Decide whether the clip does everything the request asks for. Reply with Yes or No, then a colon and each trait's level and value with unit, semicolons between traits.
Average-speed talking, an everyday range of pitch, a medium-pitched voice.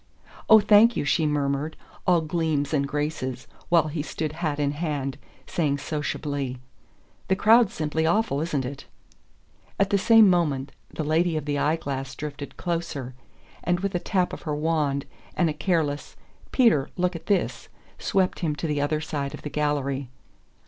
Yes: average, 170 wpm; average, 3.4 semitones; medium, 155 Hz